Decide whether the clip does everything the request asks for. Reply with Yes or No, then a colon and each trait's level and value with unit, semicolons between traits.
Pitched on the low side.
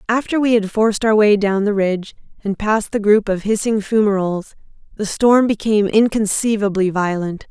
No: high, 210 Hz